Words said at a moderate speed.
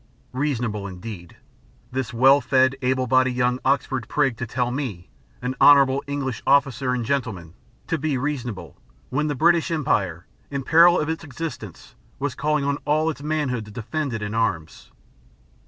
Yes: average, 160 wpm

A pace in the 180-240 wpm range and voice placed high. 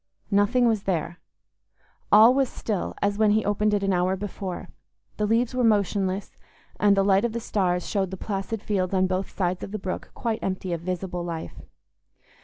Yes: average, 190 wpm; high, 195 Hz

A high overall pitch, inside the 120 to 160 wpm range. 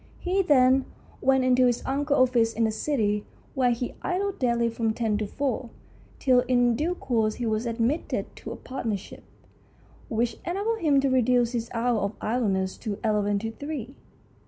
No: high, 245 Hz; average, 170 wpm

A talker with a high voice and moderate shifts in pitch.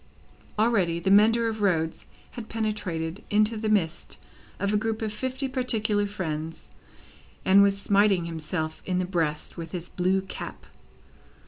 Yes: high, 200 Hz; average, 4.2 semitones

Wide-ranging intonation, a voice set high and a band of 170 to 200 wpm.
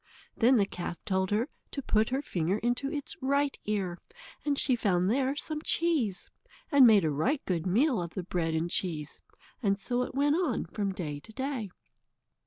Yes: wide, 7.0 semitones; high, 215 Hz; average, 190 wpm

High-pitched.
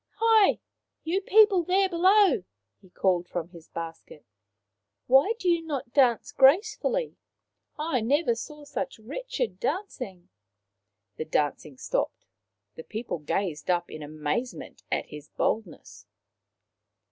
Yes: high, 245 Hz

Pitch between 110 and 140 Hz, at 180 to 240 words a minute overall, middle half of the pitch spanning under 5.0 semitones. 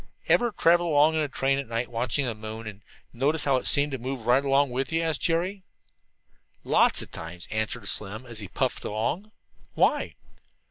No: low, 135 Hz; average, 190 wpm; average, 5.3 semitones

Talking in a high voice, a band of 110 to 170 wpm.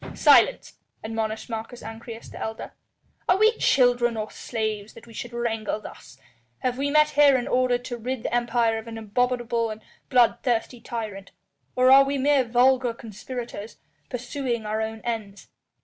Yes: high, 235 Hz; average, 160 wpm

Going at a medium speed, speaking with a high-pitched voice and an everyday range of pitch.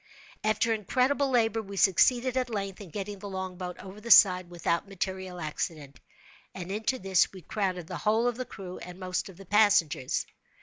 Yes: average, 180 wpm; high, 195 Hz; average, 3.3 semitones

